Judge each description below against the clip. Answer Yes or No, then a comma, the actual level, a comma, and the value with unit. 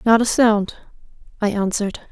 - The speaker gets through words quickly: No, average, 140 wpm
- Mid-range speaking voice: No, high, 215 Hz